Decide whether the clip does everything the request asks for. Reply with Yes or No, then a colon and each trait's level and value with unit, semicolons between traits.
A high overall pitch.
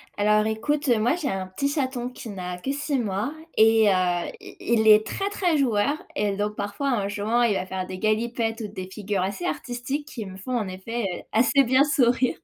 Yes: high, 220 Hz